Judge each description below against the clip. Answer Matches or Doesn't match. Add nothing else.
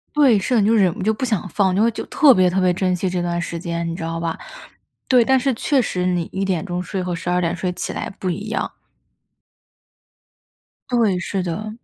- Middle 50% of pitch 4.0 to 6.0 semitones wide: Doesn't match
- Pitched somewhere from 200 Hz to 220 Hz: Doesn't match